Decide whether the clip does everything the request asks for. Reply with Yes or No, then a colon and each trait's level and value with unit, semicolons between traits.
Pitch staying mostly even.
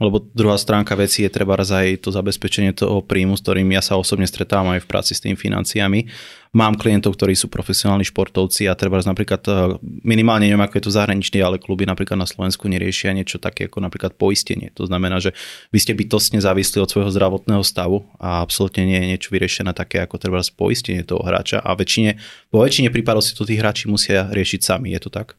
Yes: narrow, 1.8 semitones